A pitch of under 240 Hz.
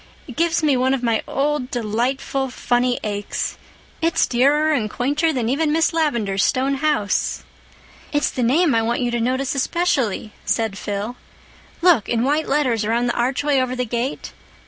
No: very high, 255 Hz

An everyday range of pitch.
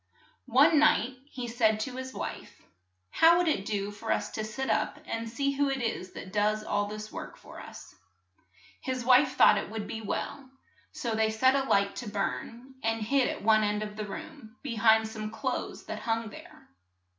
Yes: average, 3.5 semitones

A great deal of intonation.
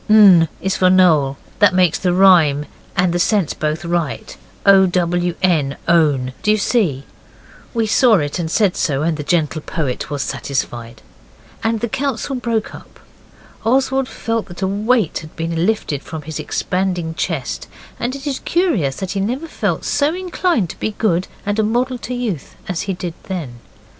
Yes: wide, 5.7 semitones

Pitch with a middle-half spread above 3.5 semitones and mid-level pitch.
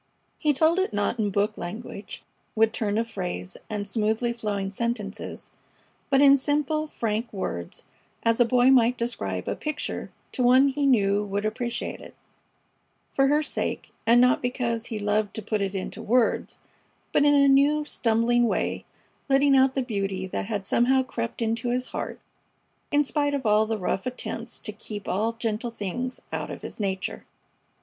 No: average, 3.9 semitones; high, 230 Hz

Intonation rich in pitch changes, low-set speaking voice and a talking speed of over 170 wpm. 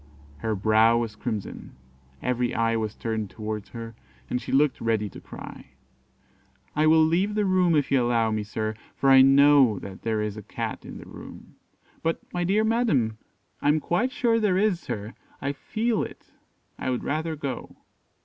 Yes: wide, 6.9 semitones; low, 130 Hz; average, 190 wpm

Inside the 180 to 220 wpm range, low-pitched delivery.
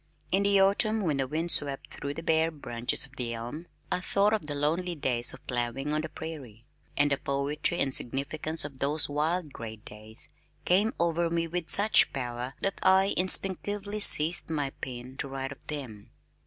No: average, 185 wpm; medium, 150 Hz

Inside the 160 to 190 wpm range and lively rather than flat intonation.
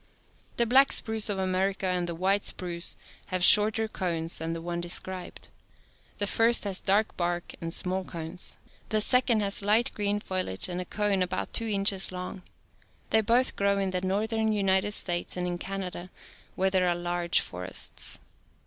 No: average, 165 wpm; average, 2.8 semitones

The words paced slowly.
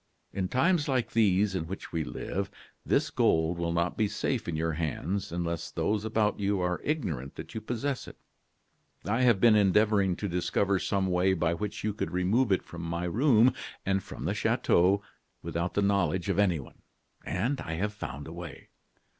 No: average, 185 wpm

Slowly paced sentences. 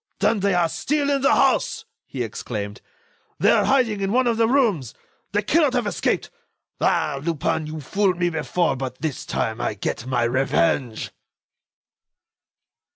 No: average, 155 wpm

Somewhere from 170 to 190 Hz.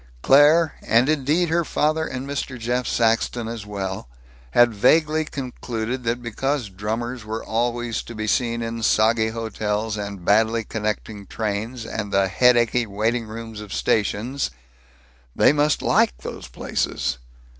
No: low, 115 Hz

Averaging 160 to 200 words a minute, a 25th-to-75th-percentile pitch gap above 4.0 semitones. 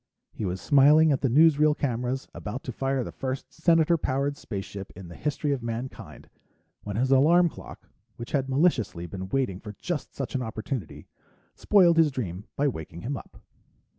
Yes: average, 175 wpm; average, 5.1 semitones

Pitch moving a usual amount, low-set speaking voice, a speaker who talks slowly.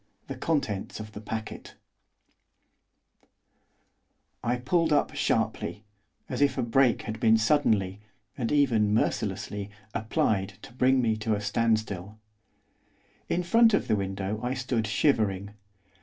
Yes: average, 3.8 semitones; low, 110 Hz; slow, 125 wpm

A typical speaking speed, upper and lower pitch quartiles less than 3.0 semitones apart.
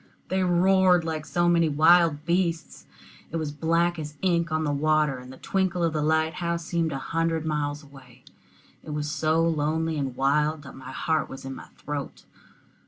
Yes: average, 190 wpm; narrow, 2.4 semitones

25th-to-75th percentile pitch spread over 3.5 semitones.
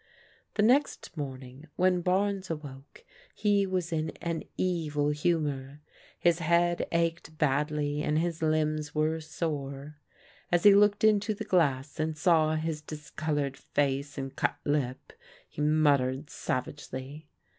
No: average, 2.9 semitones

